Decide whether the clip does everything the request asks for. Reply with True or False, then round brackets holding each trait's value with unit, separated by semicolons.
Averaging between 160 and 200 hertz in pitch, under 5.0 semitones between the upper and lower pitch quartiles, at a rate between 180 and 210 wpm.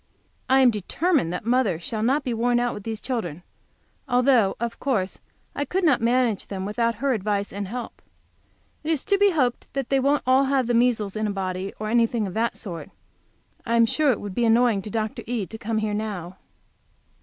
False (230 Hz; 3.7 semitones; 205 wpm)